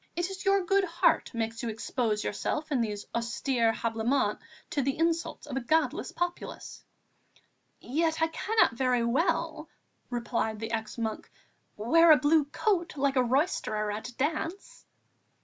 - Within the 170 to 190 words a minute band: No, average, 150 wpm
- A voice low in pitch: No, very high, 270 Hz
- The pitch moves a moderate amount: No, wide, 6.1 semitones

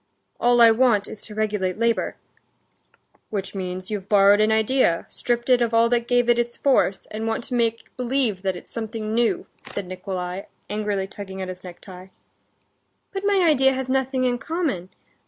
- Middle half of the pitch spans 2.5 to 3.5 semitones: No, average, 3.9 semitones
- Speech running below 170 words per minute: No, average, 175 wpm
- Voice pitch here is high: Yes, high, 220 Hz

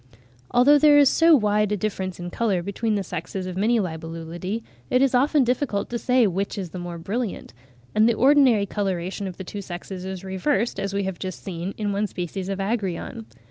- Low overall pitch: No, high, 200 Hz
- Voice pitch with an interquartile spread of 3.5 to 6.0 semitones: Yes, average, 4.1 semitones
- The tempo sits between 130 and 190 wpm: No, fast, 205 wpm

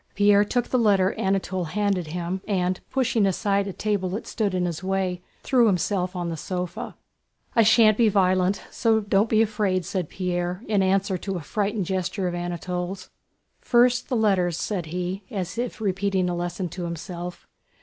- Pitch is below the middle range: No, high, 190 Hz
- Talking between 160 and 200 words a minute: Yes, average, 170 wpm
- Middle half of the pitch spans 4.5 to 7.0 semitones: No, narrow, 2.5 semitones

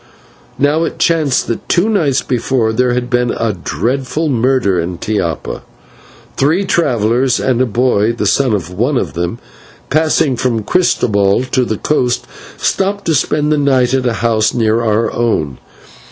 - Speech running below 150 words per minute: No, average, 165 wpm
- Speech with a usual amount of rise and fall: Yes, average, 4.3 semitones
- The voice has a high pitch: No, low, 125 Hz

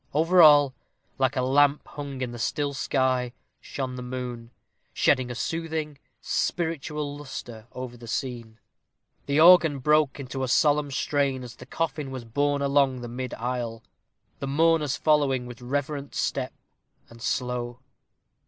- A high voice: No, low, 135 Hz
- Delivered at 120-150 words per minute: Yes, average, 145 wpm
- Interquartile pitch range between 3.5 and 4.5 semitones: No, average, 2.9 semitones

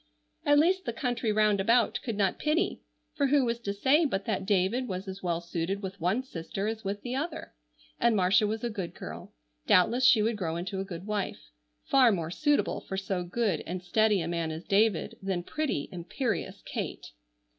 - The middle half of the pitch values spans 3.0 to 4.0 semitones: No, average, 4.6 semitones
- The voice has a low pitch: No, high, 205 Hz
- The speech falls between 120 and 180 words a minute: No, average, 200 wpm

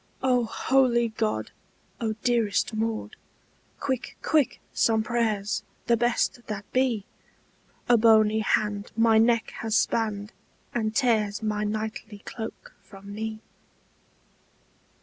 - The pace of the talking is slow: Yes, slow, 110 wpm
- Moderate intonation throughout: No, narrow, 1.9 semitones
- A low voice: No, high, 220 Hz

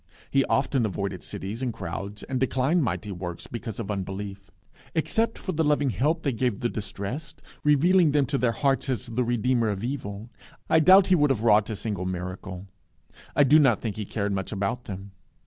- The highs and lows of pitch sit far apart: Yes, wide, 5.8 semitones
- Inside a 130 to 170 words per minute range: No, average, 200 wpm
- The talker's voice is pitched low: Yes, low, 115 Hz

